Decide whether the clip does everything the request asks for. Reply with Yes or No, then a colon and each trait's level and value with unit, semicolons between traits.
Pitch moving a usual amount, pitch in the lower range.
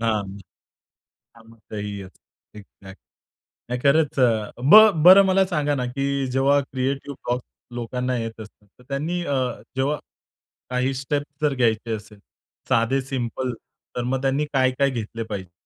Yes: average, 3.5 semitones; low, 130 Hz